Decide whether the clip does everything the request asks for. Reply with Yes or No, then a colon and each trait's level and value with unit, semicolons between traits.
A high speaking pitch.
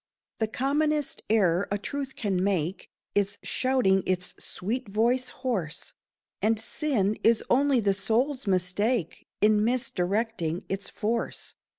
Yes: high, 215 Hz